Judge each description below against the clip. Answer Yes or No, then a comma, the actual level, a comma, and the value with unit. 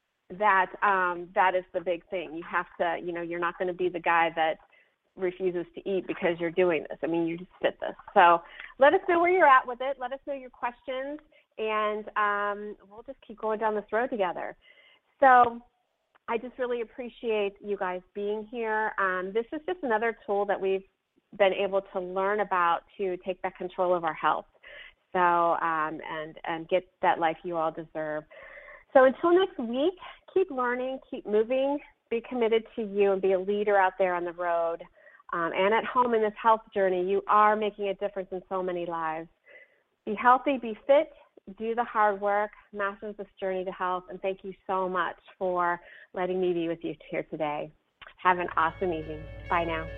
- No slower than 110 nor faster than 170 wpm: No, average, 200 wpm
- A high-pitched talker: Yes, high, 200 Hz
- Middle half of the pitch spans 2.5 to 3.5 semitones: No, average, 4.4 semitones